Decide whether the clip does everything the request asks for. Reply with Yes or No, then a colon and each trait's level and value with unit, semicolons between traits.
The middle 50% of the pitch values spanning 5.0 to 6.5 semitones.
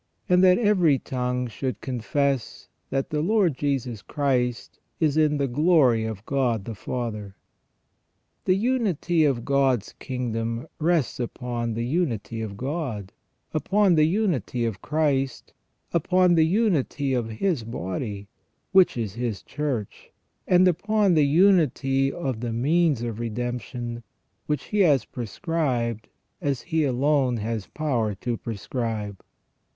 Yes: wide, 5.5 semitones